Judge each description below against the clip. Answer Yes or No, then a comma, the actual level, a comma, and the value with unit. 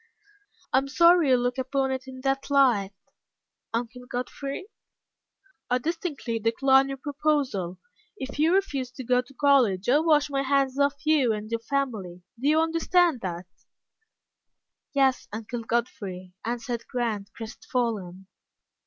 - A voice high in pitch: Yes, very high, 260 Hz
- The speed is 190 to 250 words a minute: No, slow, 135 wpm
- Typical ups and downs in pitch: Yes, average, 3.5 semitones